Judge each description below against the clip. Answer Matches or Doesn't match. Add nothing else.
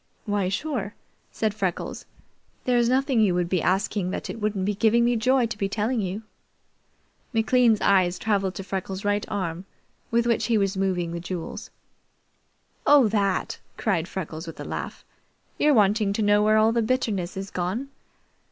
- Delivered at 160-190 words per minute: Matches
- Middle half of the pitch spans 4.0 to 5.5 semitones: Doesn't match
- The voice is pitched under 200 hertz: Doesn't match